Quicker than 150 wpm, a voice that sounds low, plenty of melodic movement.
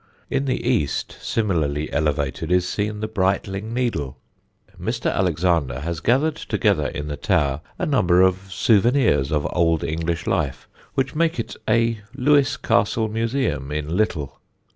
No: average, 140 wpm; very low, 95 Hz; wide, 7.2 semitones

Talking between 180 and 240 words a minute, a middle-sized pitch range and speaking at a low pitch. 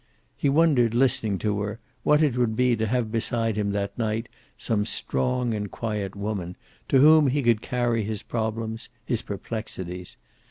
No: average, 165 wpm; average, 3.0 semitones; low, 115 Hz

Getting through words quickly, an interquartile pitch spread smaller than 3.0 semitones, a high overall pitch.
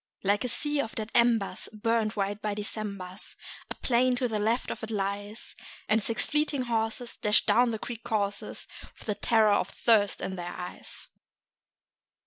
No: average, 170 wpm; narrow, 2.5 semitones; high, 220 Hz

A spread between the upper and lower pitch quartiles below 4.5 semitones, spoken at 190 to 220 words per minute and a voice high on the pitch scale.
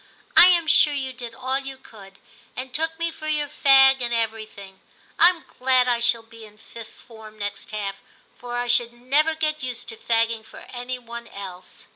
Yes: average, 3.3 semitones; average, 195 wpm; high, 245 Hz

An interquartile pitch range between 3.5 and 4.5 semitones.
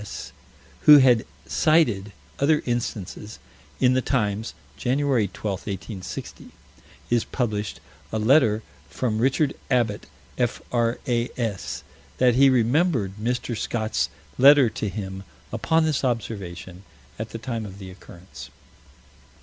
Yes: average, 3.8 semitones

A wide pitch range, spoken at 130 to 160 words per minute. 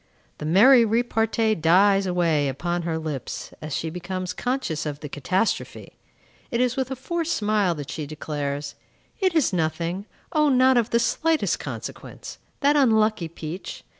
Yes: wide, 7.3 semitones; average, 155 wpm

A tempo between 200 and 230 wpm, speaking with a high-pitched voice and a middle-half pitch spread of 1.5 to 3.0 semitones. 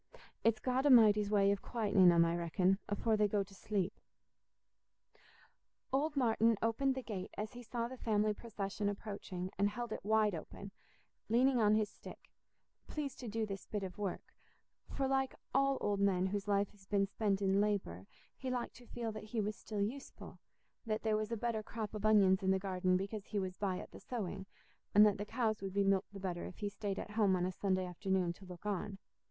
Yes: fast, 205 wpm; high, 205 Hz; narrow, 2.4 semitones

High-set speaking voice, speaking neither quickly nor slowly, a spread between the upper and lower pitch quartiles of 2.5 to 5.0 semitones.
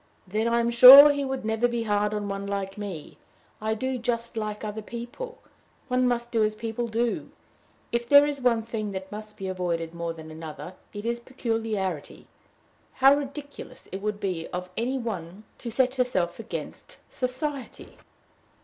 Yes: high, 225 Hz; average, 170 wpm; average, 3.8 semitones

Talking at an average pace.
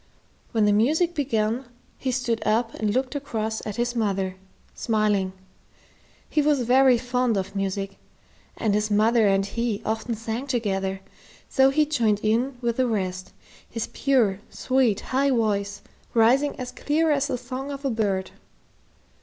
Yes: average, 155 wpm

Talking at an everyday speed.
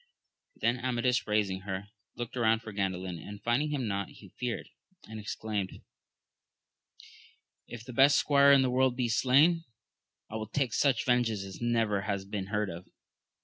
Yes: average, 165 wpm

